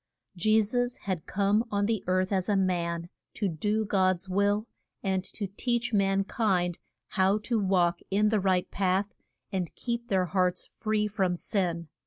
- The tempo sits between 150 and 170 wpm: Yes, average, 165 wpm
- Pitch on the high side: Yes, high, 195 Hz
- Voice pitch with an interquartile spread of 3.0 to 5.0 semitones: No, narrow, 2.4 semitones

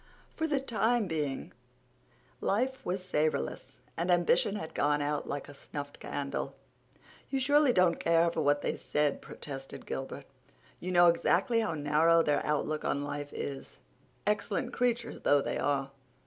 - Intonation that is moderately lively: No, wide, 6.3 semitones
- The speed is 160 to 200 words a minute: No, average, 150 wpm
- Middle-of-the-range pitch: Yes, medium, 165 Hz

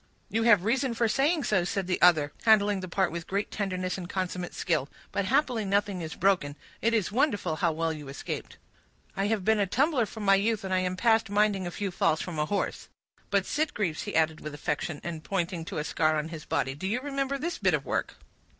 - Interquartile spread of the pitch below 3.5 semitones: No, average, 4.7 semitones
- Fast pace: Yes, fast, 225 wpm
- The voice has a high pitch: Yes, high, 195 Hz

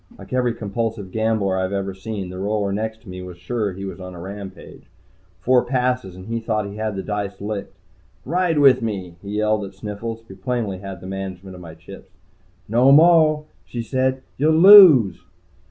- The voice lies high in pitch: No, low, 105 Hz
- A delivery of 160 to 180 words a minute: No, average, 190 wpm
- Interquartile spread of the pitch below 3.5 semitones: No, average, 4.2 semitones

